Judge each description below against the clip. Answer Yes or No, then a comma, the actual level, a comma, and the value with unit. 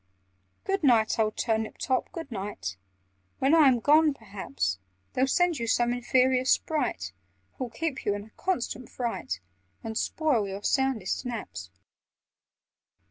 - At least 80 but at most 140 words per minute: Yes, slow, 135 wpm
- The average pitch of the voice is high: Yes, high, 240 Hz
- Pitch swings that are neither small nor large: Yes, average, 4.6 semitones